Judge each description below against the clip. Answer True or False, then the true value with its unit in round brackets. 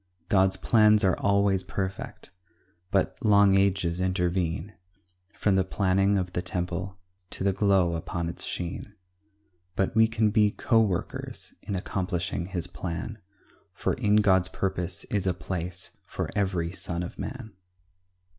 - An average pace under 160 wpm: True (140 wpm)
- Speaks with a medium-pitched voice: False (95 Hz)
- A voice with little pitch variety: True (2.2 semitones)